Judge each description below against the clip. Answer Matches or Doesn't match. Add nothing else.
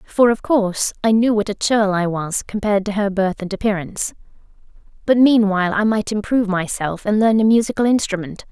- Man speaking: Doesn't match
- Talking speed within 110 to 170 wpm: Doesn't match